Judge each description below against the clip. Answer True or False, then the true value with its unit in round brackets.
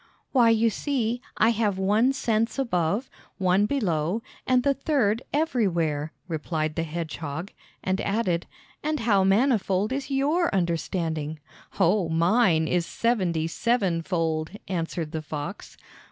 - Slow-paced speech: True (125 wpm)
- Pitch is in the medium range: False (195 Hz)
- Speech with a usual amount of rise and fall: False (6.0 semitones)